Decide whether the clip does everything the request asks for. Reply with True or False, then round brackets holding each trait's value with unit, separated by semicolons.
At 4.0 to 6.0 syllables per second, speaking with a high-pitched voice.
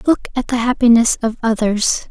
True (5.0 syllables/s; 235 Hz)